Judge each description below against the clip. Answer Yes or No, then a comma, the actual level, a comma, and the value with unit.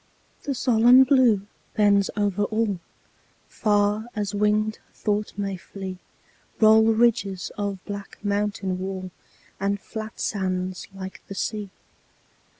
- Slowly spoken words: Yes, slow, 115 wpm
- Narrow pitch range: Yes, narrow, 1.9 semitones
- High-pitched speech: Yes, high, 205 Hz